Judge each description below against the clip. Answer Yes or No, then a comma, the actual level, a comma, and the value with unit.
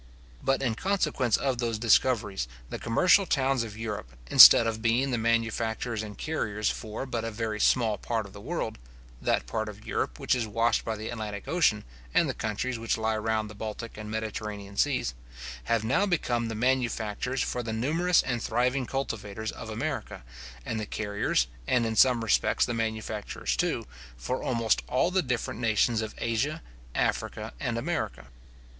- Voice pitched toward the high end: No, low, 115 Hz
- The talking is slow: No, average, 175 wpm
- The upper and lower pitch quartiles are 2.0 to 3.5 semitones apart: Yes, narrow, 2.6 semitones